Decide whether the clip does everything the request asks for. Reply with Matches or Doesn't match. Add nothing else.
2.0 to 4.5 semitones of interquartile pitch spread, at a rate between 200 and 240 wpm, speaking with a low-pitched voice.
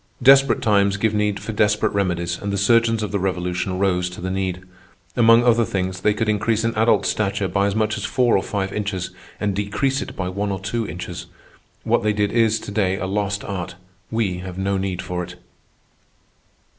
Matches